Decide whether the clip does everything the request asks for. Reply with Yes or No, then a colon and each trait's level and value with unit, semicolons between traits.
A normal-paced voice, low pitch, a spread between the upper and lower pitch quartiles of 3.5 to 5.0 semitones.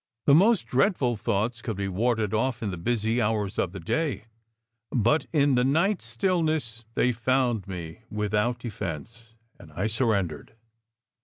Yes: average, 155 wpm; low, 115 Hz; average, 4.0 semitones